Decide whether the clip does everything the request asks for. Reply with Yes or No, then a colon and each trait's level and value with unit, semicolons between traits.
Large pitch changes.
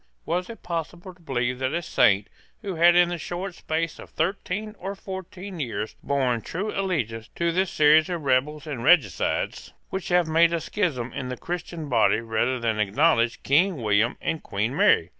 Yes: wide, 6.1 semitones